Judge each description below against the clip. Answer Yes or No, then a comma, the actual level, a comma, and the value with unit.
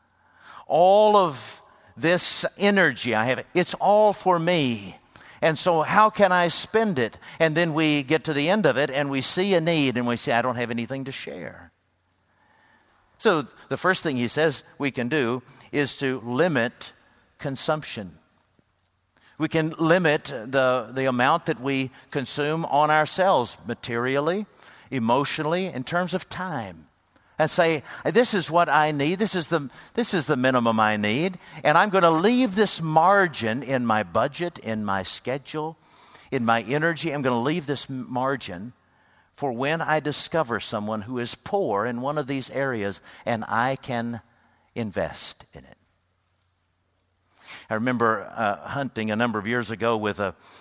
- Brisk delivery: No, average, 165 wpm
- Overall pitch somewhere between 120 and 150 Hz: Yes, medium, 140 Hz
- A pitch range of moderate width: No, wide, 6.1 semitones